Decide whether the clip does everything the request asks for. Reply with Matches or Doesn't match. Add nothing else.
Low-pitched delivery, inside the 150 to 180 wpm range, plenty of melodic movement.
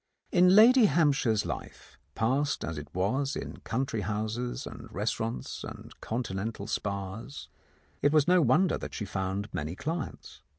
Doesn't match